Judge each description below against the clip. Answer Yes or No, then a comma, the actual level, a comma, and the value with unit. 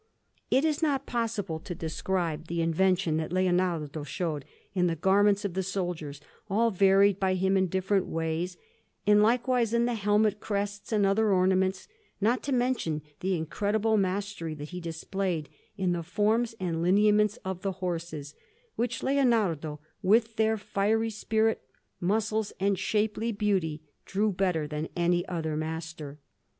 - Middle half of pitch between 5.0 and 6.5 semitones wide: No, average, 4.0 semitones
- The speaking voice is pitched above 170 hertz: Yes, high, 190 Hz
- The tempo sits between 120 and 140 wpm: No, average, 150 wpm